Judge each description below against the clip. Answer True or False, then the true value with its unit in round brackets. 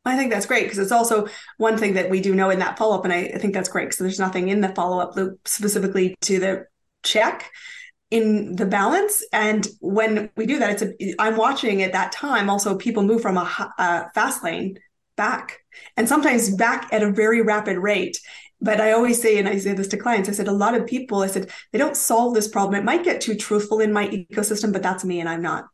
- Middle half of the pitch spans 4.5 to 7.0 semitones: False (2.8 semitones)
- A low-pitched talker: False (210 Hz)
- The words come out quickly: True (245 wpm)